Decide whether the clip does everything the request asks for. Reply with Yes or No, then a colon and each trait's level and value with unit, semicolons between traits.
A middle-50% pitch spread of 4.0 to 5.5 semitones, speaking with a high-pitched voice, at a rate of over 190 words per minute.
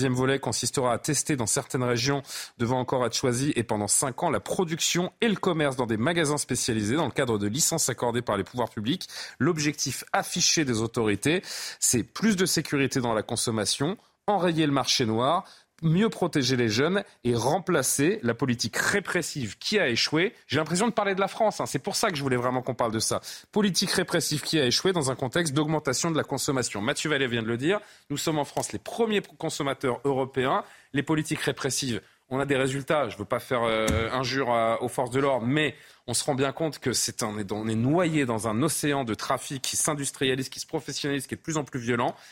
No: average, 4.7 semitones; medium, 140 Hz; fast, 220 wpm